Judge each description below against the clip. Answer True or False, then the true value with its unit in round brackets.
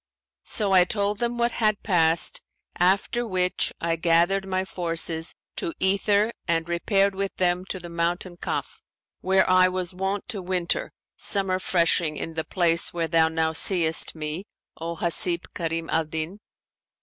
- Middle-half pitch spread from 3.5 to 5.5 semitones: False (2.7 semitones)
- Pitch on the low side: False (180 Hz)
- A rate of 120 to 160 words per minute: True (155 wpm)